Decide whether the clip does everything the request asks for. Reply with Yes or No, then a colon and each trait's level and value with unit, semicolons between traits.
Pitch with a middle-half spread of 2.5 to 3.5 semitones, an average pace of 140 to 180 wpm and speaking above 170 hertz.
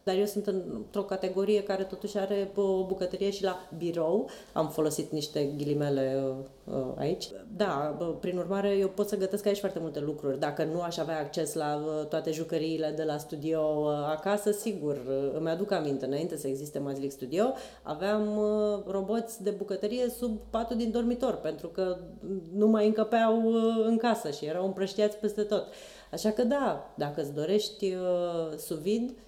No: average, 5.2 semitones; average, 160 wpm; high, 190 Hz